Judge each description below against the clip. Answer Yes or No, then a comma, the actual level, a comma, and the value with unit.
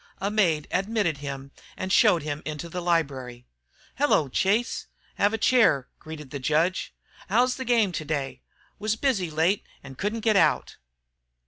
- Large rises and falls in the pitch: Yes, wide, 6.6 semitones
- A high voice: No, medium, 170 Hz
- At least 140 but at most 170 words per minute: Yes, average, 150 wpm